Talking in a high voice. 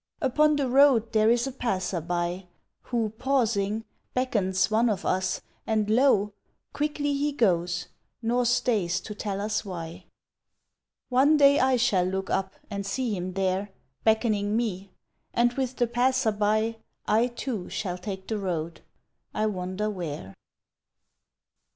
Yes: high, 215 Hz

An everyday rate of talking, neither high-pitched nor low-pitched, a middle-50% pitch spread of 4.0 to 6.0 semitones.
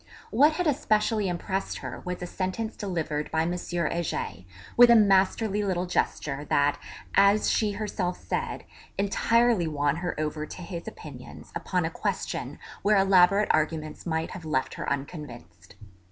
Yes: average, 150 wpm; medium, 180 Hz; average, 4.7 semitones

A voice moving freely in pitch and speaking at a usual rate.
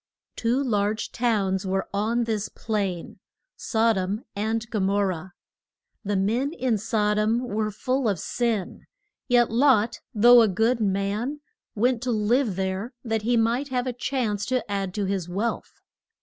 No: average, 3.2 semitones; average, 160 wpm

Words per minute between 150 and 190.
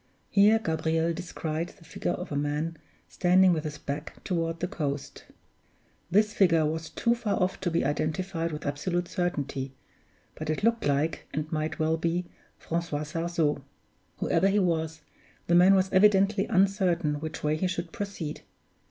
Yes: average, 160 wpm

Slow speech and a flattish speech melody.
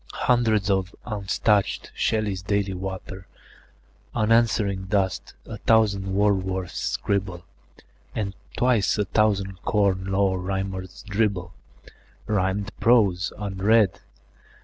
Yes: slow, 95 wpm; narrow, 2.0 semitones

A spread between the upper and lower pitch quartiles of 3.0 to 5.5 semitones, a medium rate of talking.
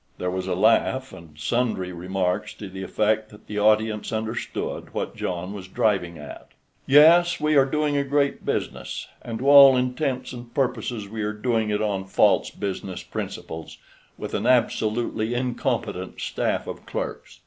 Yes: average, 5.1 semitones; average, 165 wpm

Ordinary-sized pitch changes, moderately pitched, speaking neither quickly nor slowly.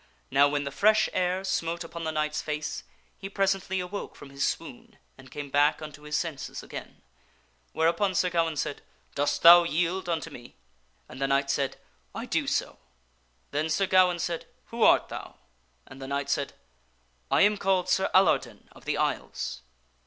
Yes: average, 4.6 semitones; medium, 160 Hz; average, 180 wpm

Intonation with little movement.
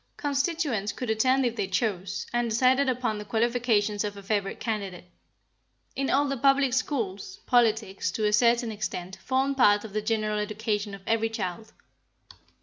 No: average, 3.6 semitones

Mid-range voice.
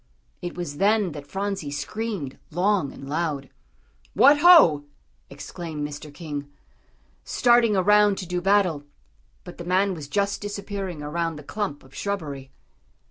Yes: medium, 175 Hz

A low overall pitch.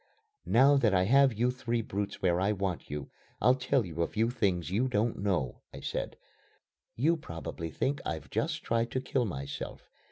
Yes: low, 110 Hz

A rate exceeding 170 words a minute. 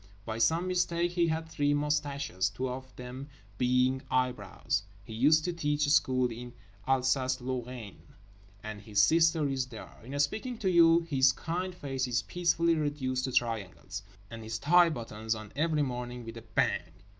No: average, 165 wpm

